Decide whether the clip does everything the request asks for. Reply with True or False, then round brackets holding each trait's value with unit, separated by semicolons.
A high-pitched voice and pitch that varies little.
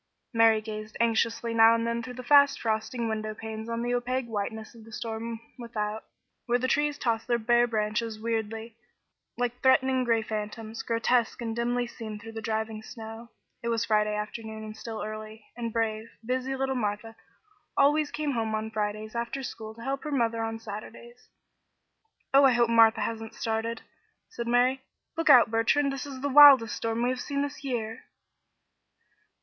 True (230 Hz; 1.9 semitones)